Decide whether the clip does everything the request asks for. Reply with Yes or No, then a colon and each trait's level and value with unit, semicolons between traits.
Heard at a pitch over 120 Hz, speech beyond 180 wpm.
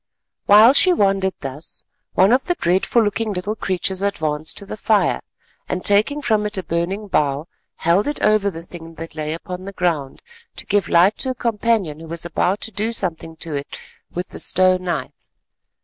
Yes: high, 190 Hz; average, 190 wpm